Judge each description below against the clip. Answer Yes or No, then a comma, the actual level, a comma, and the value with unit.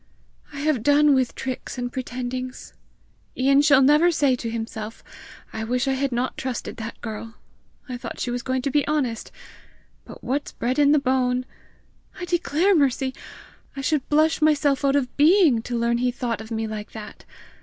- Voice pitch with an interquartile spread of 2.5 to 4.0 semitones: Yes, average, 3.1 semitones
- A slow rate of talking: No, average, 185 wpm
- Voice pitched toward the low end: No, very high, 260 Hz